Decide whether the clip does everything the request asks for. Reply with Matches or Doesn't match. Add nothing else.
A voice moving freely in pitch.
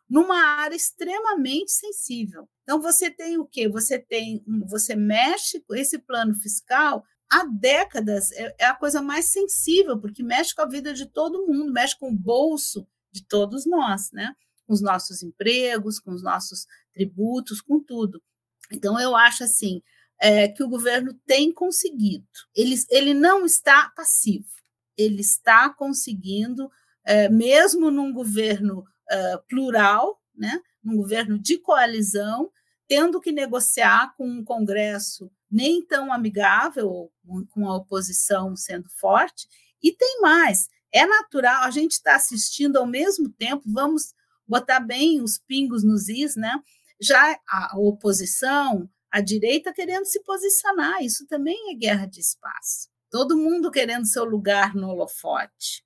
Matches